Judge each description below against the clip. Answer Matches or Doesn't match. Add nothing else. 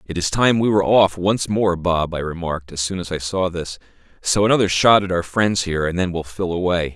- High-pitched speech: Doesn't match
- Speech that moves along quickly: Matches